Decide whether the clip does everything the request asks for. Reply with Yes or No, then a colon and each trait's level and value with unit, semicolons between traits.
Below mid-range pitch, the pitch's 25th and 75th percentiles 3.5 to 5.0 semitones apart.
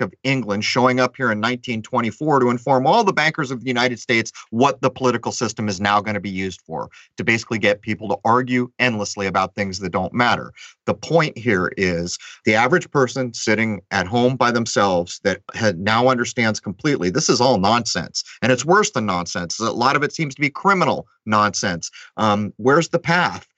Yes: low, 120 Hz; average, 3.9 semitones